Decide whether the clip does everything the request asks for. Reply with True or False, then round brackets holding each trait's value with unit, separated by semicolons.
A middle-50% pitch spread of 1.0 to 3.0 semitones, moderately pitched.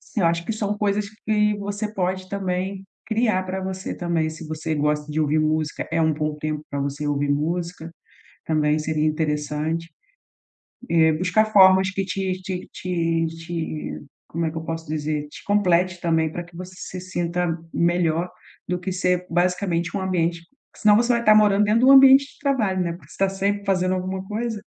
False (3.4 semitones; 180 Hz)